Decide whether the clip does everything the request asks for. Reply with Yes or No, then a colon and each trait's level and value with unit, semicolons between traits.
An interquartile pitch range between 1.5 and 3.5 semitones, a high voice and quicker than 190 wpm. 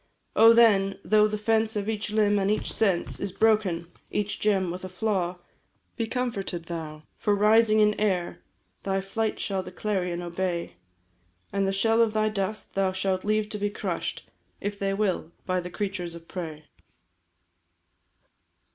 No: average, 2.7 semitones; high, 200 Hz; average, 165 wpm